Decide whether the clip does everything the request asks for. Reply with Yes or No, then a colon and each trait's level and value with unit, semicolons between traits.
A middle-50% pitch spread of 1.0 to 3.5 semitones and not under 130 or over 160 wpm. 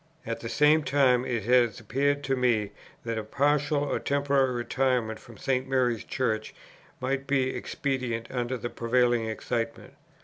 Yes: average, 2.9 semitones; average, 150 wpm